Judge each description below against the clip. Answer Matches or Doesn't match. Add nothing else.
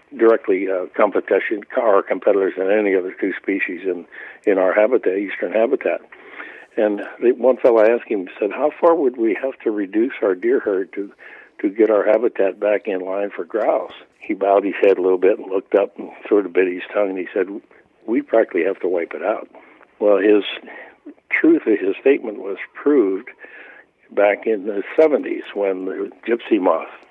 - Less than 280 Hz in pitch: Doesn't match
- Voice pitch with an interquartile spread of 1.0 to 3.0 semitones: Doesn't match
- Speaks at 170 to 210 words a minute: Matches